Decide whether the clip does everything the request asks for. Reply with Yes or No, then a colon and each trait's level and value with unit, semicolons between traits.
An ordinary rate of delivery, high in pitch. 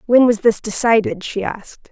Yes: average, 190 wpm; high, 220 Hz